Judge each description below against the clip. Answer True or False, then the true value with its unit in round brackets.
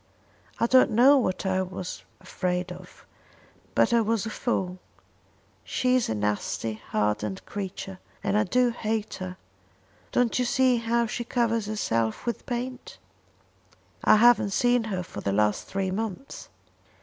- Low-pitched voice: False (210 Hz)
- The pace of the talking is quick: False (150 wpm)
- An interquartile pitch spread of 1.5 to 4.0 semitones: False (4.7 semitones)